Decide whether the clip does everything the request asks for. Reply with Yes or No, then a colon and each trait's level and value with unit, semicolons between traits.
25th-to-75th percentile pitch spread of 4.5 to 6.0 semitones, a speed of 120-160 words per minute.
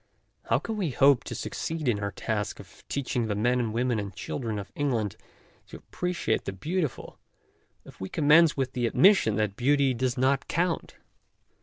No: average, 5.0 semitones; average, 185 wpm